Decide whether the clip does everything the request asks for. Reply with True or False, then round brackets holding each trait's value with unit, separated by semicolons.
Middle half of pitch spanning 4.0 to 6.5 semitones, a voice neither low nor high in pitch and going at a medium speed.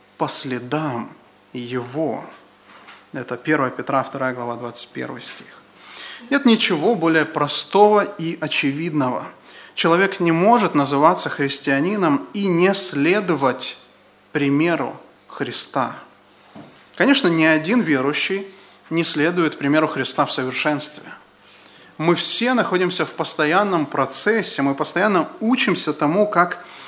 False (5.1 semitones; 160 Hz; 105 wpm)